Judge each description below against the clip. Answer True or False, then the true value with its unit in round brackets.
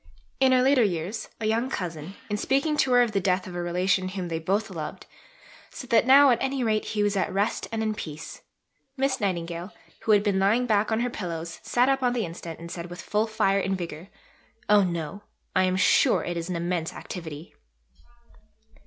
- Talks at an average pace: False (210 wpm)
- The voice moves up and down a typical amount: True (4.7 semitones)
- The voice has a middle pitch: False (195 Hz)